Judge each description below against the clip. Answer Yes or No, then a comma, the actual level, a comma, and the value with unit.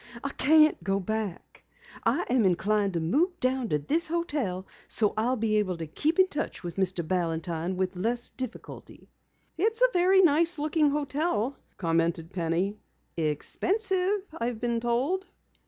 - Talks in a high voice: Yes, high, 235 Hz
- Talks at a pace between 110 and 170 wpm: Yes, average, 150 wpm